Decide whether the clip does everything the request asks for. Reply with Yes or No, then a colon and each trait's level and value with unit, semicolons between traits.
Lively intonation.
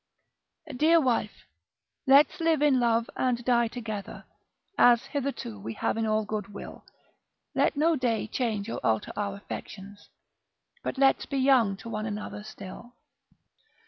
No: average, 4.2 semitones